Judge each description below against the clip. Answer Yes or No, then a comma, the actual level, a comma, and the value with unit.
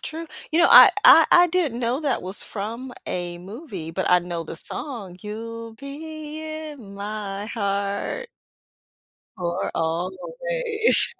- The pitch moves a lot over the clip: Yes, wide, 8.3 semitones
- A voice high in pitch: Yes, high, 220 Hz